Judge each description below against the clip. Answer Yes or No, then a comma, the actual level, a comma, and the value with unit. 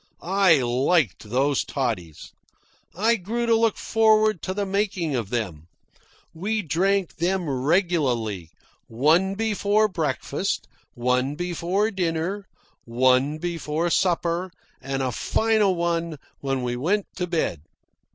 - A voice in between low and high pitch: Yes, medium, 170 Hz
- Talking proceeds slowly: Yes, slow, 120 wpm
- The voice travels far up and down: Yes, wide, 6.9 semitones